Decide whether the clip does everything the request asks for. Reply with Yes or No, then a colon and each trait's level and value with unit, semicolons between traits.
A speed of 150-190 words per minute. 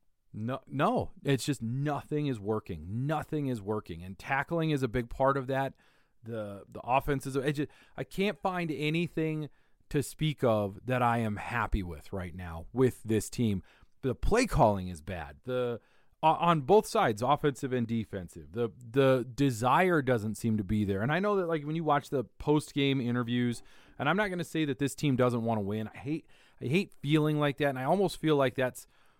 No: average, 200 wpm